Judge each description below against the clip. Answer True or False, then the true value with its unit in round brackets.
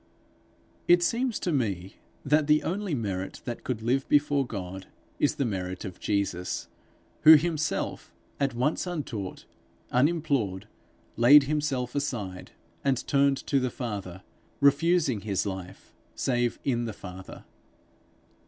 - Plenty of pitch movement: True (6.7 semitones)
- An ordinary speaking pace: False (130 wpm)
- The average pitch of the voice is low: True (125 Hz)